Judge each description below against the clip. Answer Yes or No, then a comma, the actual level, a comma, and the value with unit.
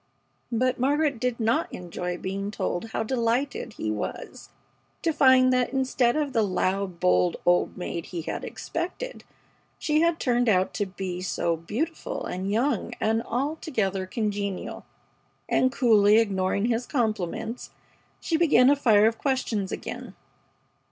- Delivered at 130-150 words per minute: Yes, average, 140 wpm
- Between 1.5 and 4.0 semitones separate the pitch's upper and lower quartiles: No, average, 5.3 semitones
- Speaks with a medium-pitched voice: No, high, 225 Hz